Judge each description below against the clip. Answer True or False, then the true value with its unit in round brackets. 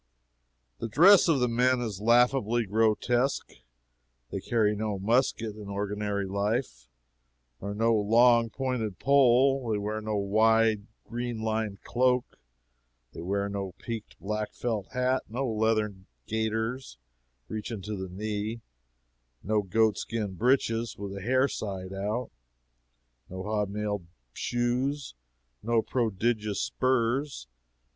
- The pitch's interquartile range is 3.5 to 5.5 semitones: False (2.9 semitones)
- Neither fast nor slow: False (120 wpm)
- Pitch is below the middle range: True (110 Hz)